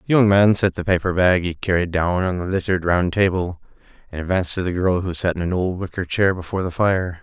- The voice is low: Yes, very low, 90 Hz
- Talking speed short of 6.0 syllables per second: No, 6.1 syllables/s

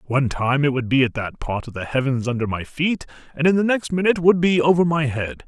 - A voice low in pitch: No, medium, 145 Hz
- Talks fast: Yes, fast, 265 wpm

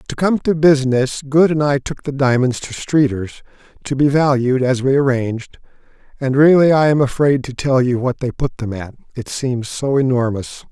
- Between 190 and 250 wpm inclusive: Yes, average, 195 wpm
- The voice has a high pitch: No, low, 135 Hz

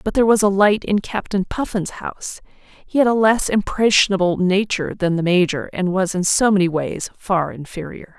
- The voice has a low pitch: No, high, 195 Hz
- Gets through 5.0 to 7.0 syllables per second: Yes, 5.1 syllables/s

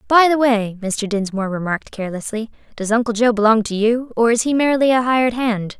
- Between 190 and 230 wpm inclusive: Yes, fast, 205 wpm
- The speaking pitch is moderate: No, high, 230 Hz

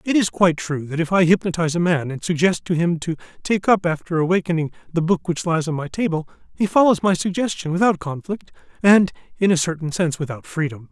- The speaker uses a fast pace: Yes, fast, 215 wpm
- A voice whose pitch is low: No, medium, 170 Hz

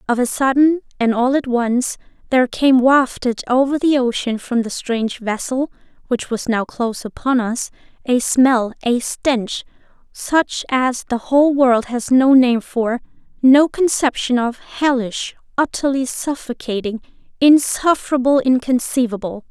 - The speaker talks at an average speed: No, slow, 125 wpm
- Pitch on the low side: No, very high, 255 Hz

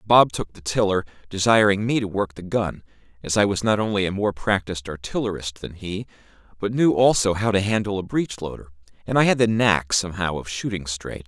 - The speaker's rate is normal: No, fast, 210 wpm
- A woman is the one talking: No, male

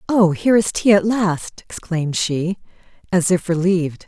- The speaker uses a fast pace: No, average, 160 wpm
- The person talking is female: Yes, female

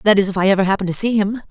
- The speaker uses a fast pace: Yes, fast, 360 wpm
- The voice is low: No, high, 200 Hz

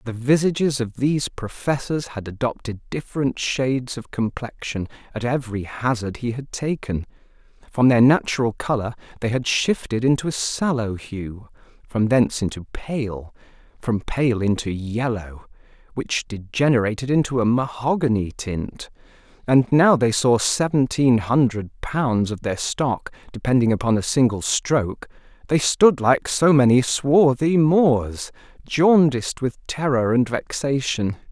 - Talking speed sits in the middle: No, slow, 130 wpm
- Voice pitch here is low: Yes, low, 125 Hz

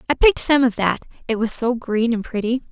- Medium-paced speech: No, fast, 245 wpm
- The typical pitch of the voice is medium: No, high, 240 Hz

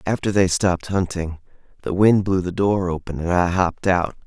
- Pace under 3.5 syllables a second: No, 5.3 syllables/s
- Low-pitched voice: Yes, very low, 90 Hz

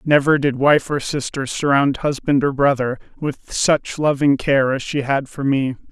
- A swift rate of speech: No, average, 185 wpm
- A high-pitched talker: No, medium, 140 Hz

